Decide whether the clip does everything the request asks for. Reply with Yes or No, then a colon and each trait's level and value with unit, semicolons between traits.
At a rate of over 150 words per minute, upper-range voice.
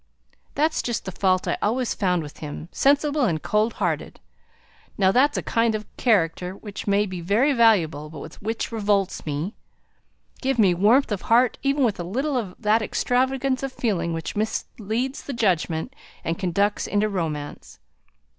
Yes: average, 165 wpm; high, 210 Hz